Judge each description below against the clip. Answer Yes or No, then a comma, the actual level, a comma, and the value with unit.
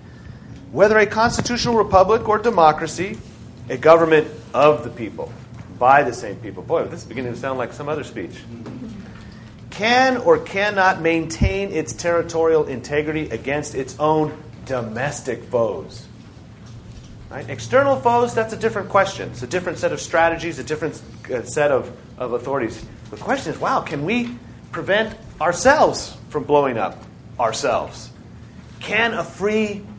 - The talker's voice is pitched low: No, medium, 150 Hz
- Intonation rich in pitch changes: Yes, wide, 7.9 semitones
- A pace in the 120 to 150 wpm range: Yes, average, 140 wpm